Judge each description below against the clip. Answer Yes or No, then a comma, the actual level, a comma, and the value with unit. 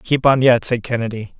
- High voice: No, low, 120 Hz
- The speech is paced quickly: Yes, fast, 215 wpm